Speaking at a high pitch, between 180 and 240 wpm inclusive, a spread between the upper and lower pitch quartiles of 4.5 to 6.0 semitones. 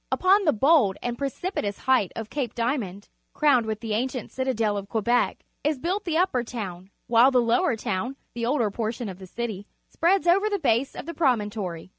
Yes: high, 240 Hz; average, 200 wpm; wide, 5.4 semitones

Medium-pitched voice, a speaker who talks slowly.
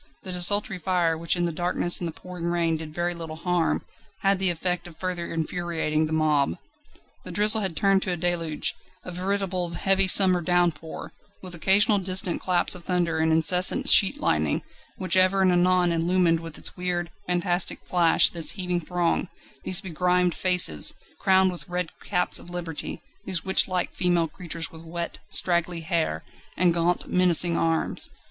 No: medium, 175 Hz; average, 165 wpm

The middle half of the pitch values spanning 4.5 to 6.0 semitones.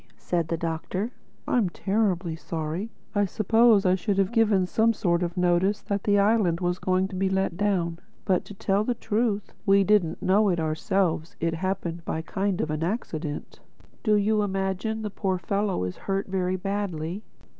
No: average, 3.0 semitones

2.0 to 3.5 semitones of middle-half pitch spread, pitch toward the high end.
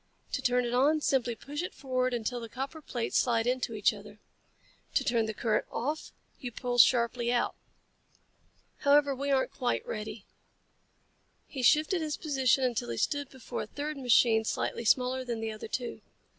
Yes: average, 2.9 semitones; very high, 250 Hz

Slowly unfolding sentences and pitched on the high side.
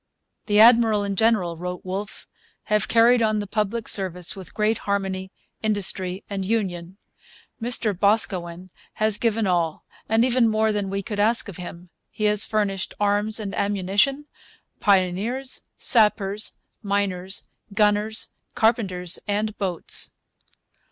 Yes: slow, 130 wpm; high, 205 Hz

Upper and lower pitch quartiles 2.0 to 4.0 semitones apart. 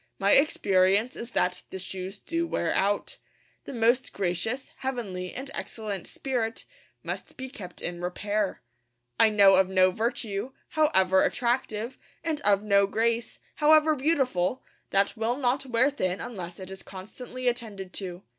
No: average, 5.0 semitones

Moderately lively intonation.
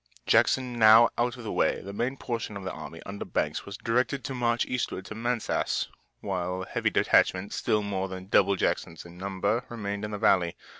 Yes: average, 3.9 semitones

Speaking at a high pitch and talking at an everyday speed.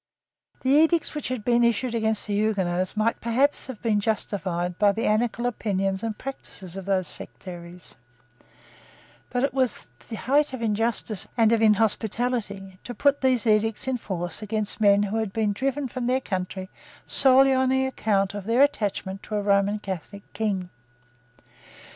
Yes: high, 220 Hz; average, 160 wpm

